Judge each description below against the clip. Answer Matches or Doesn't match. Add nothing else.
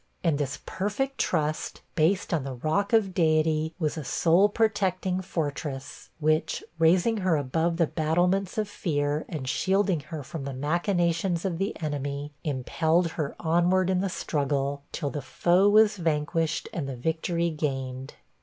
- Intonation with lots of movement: Doesn't match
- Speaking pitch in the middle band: Matches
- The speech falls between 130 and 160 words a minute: Matches